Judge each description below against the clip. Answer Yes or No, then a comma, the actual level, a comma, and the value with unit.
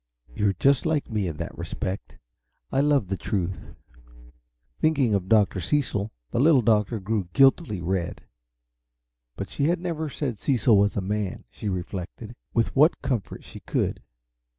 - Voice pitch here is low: Yes, low, 110 Hz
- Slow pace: No, average, 150 wpm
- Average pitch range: No, wide, 6.2 semitones